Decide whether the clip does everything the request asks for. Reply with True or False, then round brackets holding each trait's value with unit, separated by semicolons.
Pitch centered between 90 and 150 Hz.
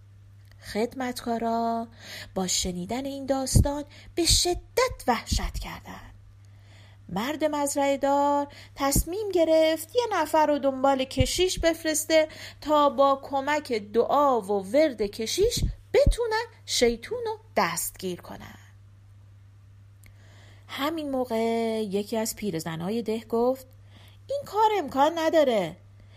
False (240 Hz)